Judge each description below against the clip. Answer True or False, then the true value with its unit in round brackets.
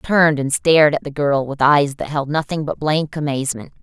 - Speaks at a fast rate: True (235 wpm)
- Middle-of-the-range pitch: True (145 Hz)